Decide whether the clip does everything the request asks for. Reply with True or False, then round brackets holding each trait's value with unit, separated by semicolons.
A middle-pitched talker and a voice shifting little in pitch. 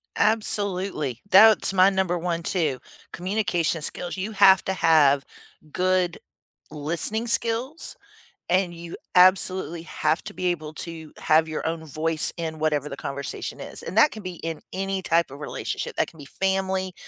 False (175 Hz; 3.3 semitones)